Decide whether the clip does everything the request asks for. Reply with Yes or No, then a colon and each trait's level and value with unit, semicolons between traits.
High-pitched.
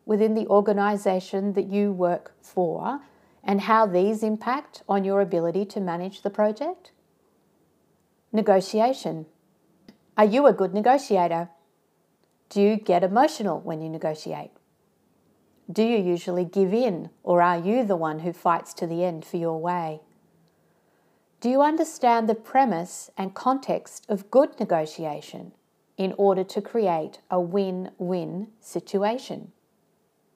Yes: high, 195 Hz